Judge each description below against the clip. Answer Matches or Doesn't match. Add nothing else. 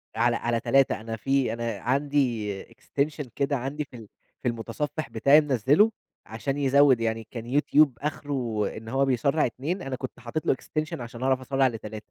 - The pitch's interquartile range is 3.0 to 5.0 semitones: Matches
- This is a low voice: Matches